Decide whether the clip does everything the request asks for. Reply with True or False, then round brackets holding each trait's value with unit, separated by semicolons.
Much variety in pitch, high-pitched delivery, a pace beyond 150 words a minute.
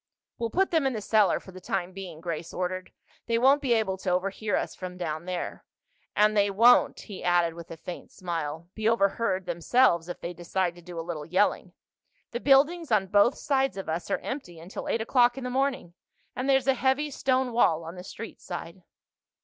True (5.9 semitones; 195 Hz; 205 wpm)